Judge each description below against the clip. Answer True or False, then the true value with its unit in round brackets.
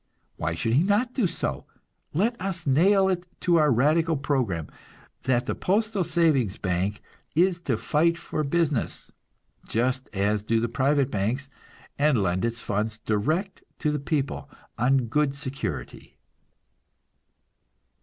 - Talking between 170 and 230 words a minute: False (135 wpm)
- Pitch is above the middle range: False (140 Hz)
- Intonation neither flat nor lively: False (6.9 semitones)